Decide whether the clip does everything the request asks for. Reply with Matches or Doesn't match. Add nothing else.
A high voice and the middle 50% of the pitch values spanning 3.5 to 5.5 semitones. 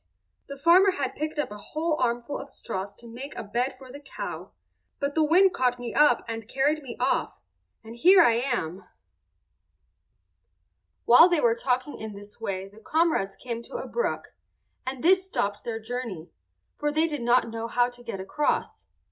Matches